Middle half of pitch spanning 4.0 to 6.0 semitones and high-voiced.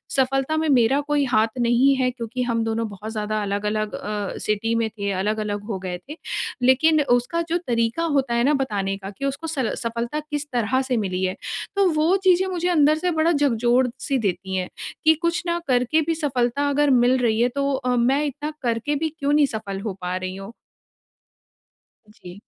Yes: average, 5.3 semitones; very high, 250 Hz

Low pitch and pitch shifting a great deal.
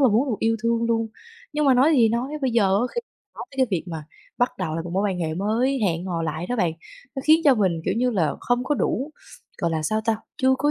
No: high, 225 Hz; wide, 6.3 semitones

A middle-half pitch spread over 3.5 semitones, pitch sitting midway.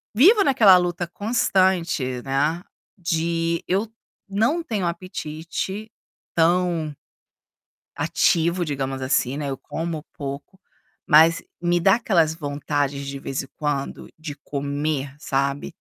Yes: average, 4.3 semitones; medium, 165 Hz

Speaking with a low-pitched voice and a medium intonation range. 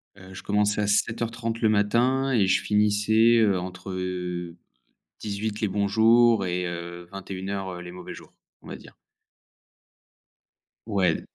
Yes: low, 100 Hz; average, 3.2 semitones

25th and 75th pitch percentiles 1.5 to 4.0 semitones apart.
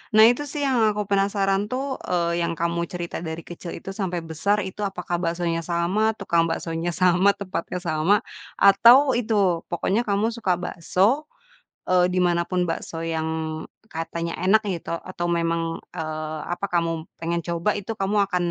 Yes: average, 2.9 semitones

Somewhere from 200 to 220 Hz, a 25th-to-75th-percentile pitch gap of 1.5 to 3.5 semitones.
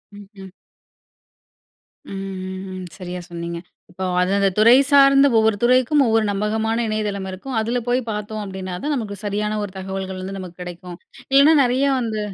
Yes: high, 205 Hz; average, 3.2 semitones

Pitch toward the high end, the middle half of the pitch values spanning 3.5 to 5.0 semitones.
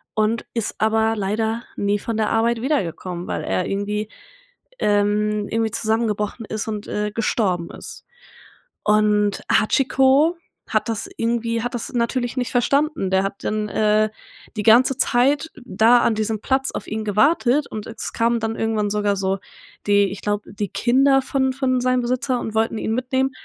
No: high, 220 Hz; average, 2.8 semitones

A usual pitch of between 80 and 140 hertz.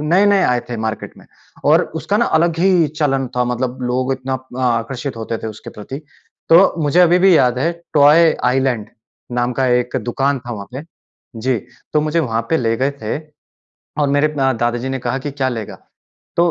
Yes: low, 135 Hz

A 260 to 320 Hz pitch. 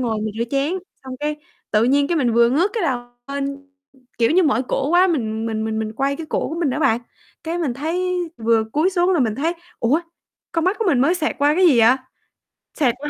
Yes: very high, 280 Hz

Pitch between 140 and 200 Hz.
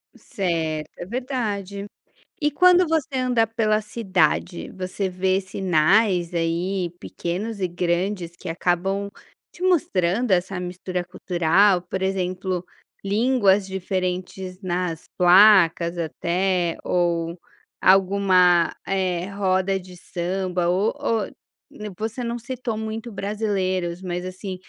Yes: high, 190 Hz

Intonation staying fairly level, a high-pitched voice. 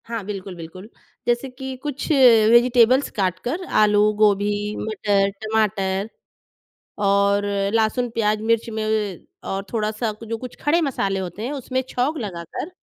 No: average, 3.4 semitones; high, 215 Hz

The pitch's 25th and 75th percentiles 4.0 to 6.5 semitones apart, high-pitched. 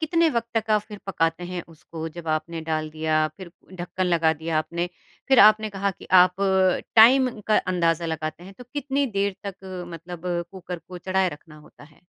No: average, 4.5 semitones; medium, 180 Hz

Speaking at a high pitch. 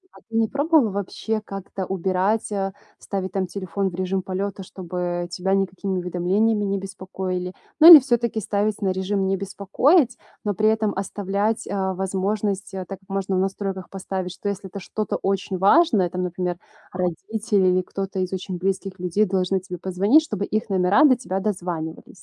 Yes: high, 195 Hz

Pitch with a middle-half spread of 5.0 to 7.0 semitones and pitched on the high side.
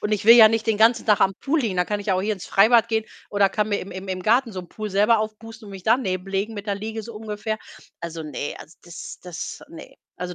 No: average, 2.8 semitones; high, 210 Hz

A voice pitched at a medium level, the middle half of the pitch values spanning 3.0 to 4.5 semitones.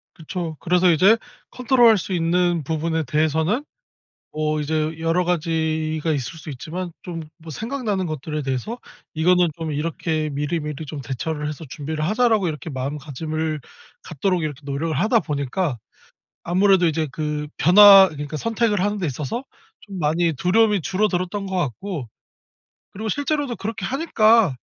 Yes: medium, 165 Hz; average, 4.2 semitones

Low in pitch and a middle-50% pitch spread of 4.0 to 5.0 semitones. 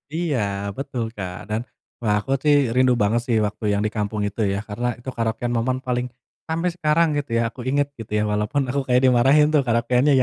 Yes: low, 125 Hz; average, 4.4 semitones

